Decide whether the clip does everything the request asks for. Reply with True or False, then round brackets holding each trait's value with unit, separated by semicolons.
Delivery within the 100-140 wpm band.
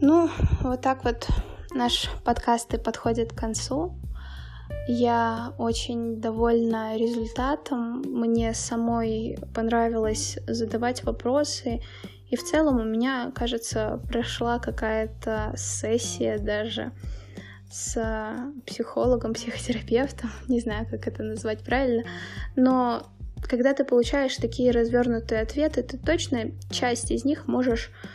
True (110 wpm)